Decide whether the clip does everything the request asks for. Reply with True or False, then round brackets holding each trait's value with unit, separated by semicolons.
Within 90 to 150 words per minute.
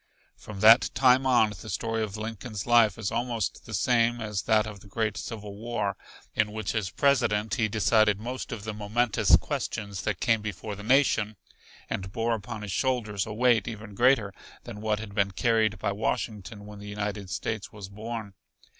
False (185 wpm)